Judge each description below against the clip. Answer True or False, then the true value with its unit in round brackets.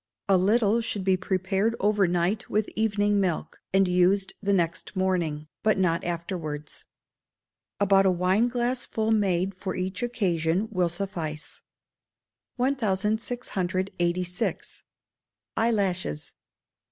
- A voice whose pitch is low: False (190 Hz)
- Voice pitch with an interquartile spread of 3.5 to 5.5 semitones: False (2.9 semitones)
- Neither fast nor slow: False (105 wpm)